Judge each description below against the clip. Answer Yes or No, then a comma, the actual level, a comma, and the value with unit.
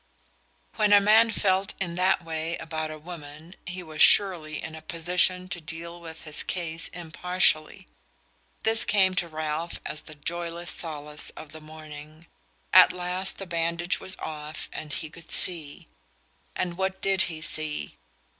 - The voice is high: No, medium, 170 Hz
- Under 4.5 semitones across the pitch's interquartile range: Yes, average, 2.7 semitones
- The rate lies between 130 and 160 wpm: Yes, average, 155 wpm